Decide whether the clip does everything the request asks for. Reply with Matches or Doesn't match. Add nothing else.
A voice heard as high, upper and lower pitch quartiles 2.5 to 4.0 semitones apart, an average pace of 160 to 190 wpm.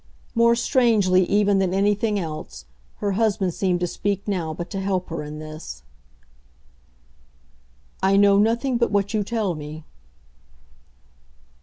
Doesn't match